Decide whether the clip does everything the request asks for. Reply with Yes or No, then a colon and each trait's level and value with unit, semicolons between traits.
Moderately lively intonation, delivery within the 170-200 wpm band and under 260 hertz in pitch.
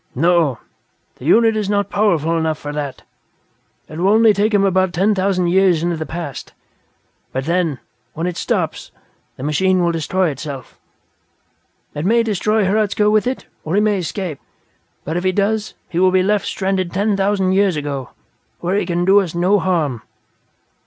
Yes: average, 3.7 semitones; average, 175 wpm; medium, 185 Hz